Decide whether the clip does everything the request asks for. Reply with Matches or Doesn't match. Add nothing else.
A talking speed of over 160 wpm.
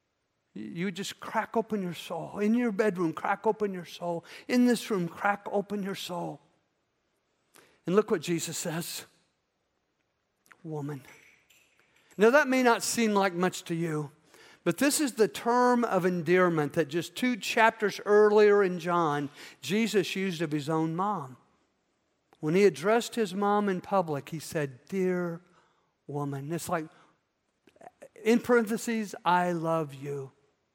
Doesn't match